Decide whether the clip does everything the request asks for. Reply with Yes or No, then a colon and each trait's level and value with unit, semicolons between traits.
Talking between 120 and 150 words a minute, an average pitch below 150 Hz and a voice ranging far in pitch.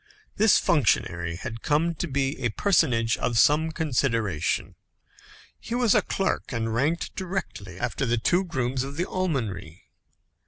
Yes: average, 145 wpm; low, 135 Hz; wide, 6.9 semitones